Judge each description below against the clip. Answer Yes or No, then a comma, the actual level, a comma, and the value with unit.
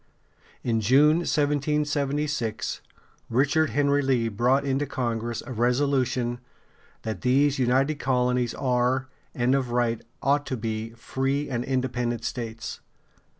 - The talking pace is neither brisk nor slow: No, slow, 115 wpm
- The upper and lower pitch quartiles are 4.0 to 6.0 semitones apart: No, average, 2.9 semitones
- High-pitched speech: No, low, 130 Hz